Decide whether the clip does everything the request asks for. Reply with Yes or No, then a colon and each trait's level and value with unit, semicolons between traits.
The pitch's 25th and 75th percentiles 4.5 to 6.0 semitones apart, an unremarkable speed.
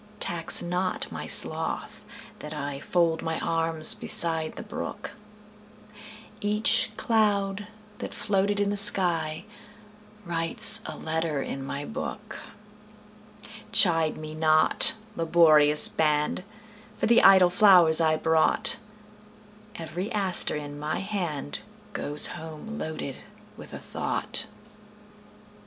No: average, 4.9 semitones; slow, 95 wpm